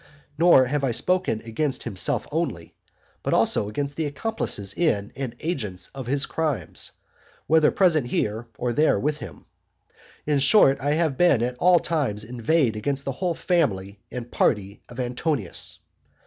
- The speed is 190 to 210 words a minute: No, average, 150 wpm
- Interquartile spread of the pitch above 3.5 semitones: Yes, wide, 5.5 semitones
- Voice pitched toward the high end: No, low, 135 Hz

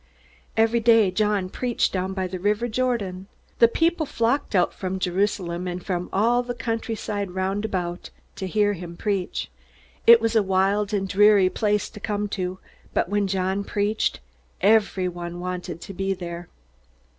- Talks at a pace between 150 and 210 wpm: Yes, average, 155 wpm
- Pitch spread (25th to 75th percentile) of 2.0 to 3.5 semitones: Yes, average, 2.9 semitones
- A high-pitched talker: Yes, high, 200 Hz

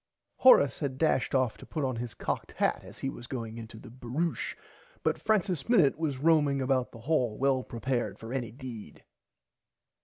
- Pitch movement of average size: Yes, average, 3.6 semitones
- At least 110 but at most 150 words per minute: No, average, 180 wpm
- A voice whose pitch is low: Yes, low, 130 Hz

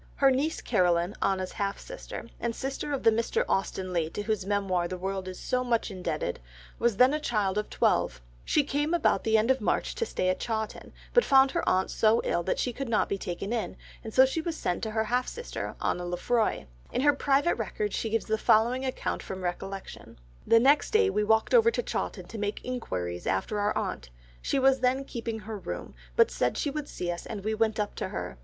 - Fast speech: Yes, fast, 225 wpm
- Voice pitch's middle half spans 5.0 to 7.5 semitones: Yes, wide, 5.6 semitones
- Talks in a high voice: Yes, high, 220 Hz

